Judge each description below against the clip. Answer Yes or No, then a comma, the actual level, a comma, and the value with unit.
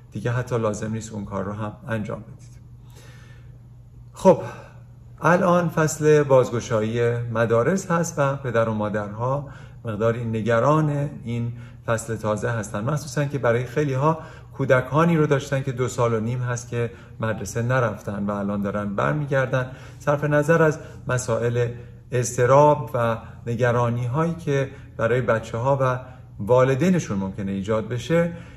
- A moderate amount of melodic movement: Yes, average, 3.0 semitones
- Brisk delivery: No, average, 135 wpm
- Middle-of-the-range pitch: No, low, 120 Hz